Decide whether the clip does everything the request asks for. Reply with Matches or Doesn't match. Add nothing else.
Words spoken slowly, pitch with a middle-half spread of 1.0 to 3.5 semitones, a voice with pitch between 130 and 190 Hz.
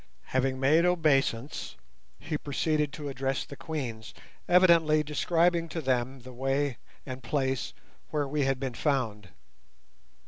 Matches